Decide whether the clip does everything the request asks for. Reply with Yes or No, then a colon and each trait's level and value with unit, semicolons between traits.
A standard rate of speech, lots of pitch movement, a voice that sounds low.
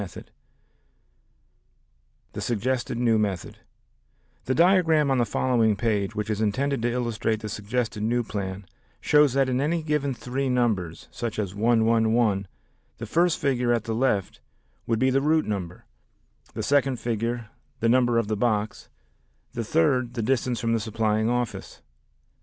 No: average, 160 wpm; average, 3.3 semitones; low, 120 Hz